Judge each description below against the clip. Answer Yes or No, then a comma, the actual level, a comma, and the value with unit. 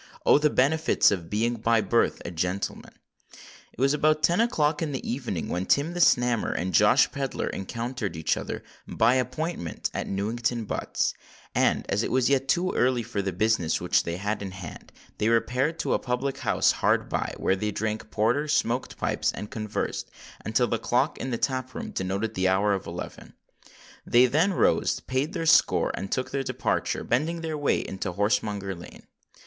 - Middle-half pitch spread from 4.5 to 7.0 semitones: Yes, wide, 5.6 semitones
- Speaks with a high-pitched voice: No, low, 120 Hz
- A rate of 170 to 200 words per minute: Yes, average, 185 wpm